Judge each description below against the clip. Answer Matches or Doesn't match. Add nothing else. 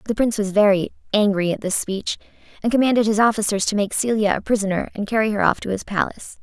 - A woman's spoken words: Matches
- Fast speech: Matches